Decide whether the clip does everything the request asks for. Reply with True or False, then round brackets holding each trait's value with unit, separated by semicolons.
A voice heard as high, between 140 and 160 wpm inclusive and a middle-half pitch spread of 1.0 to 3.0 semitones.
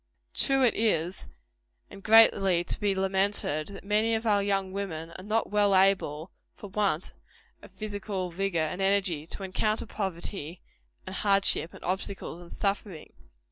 True (195 Hz; 150 wpm; 2.5 semitones)